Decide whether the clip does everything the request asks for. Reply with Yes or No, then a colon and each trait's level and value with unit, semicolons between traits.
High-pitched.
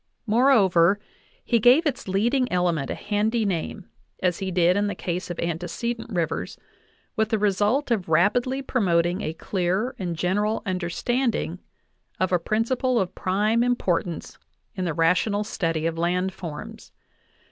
Yes: high, 195 Hz